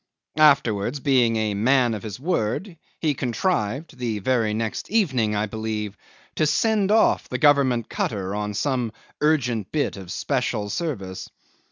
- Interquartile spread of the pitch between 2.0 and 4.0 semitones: No, wide, 5.5 semitones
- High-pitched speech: No, low, 120 Hz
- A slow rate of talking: No, average, 145 wpm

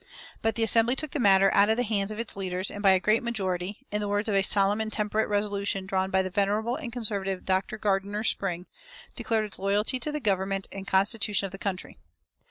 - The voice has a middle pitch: No, high, 205 Hz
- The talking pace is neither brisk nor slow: No, fast, 225 wpm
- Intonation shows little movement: Yes, narrow, 2.1 semitones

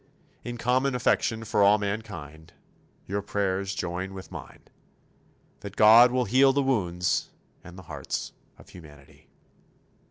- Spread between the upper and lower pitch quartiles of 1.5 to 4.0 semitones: No, average, 4.8 semitones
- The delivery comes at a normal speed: No, slow, 130 wpm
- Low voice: Yes, low, 100 Hz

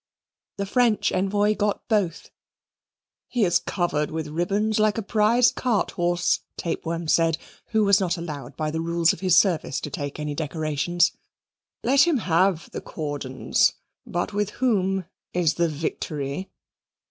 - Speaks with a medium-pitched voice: Yes, medium, 175 Hz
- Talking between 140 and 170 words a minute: Yes, average, 145 wpm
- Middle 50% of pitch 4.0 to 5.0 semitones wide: Yes, average, 4.7 semitones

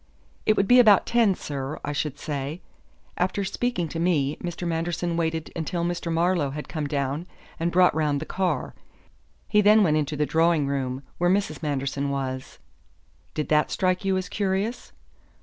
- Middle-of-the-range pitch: Yes, medium, 165 Hz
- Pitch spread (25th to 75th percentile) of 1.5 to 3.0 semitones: No, average, 4.0 semitones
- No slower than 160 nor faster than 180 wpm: Yes, average, 170 wpm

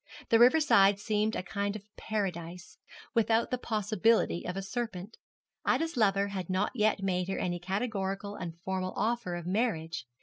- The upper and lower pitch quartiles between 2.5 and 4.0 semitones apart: Yes, average, 3.3 semitones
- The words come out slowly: No, average, 165 wpm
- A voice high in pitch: Yes, high, 200 Hz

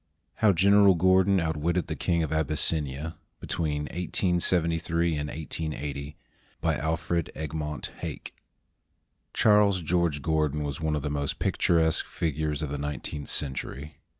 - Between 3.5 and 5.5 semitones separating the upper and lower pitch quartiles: No, narrow, 2.6 semitones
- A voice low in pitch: Yes, very low, 80 Hz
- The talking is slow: Yes, slow, 125 wpm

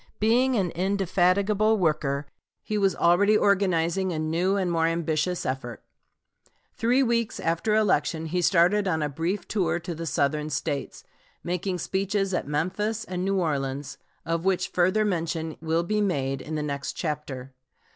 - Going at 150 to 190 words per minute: Yes, average, 155 wpm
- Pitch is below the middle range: No, medium, 175 Hz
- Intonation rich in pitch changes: No, average, 4.1 semitones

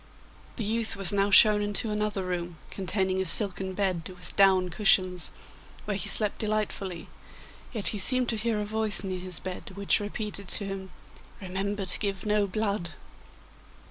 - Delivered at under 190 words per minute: Yes, average, 165 wpm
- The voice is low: No, high, 200 Hz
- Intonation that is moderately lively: No, narrow, 2.1 semitones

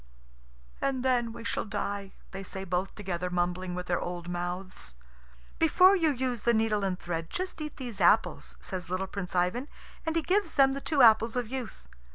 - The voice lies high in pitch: Yes, high, 210 Hz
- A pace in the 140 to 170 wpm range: No, average, 190 wpm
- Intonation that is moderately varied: No, wide, 6.4 semitones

